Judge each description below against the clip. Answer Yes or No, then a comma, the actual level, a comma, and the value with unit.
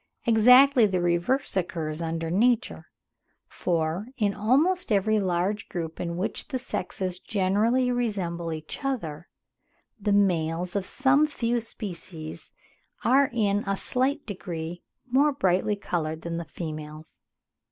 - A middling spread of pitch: No, wide, 6.0 semitones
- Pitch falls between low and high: No, high, 195 Hz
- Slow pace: Yes, slow, 125 wpm